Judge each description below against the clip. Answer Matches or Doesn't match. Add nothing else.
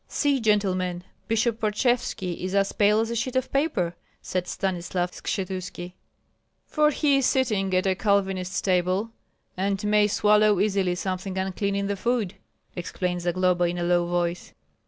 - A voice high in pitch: Matches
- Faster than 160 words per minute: Doesn't match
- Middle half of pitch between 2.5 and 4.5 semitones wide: Matches